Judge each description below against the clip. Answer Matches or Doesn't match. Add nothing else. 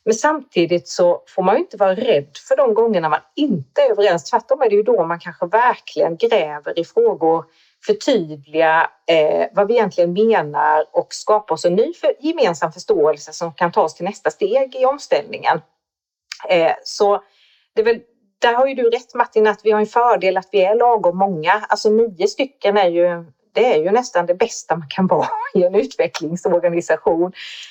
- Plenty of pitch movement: Matches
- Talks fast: Doesn't match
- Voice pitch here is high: Matches